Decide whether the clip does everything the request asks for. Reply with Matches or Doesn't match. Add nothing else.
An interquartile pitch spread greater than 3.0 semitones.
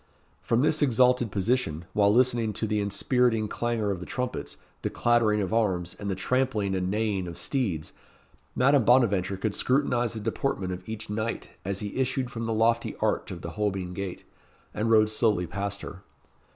Matches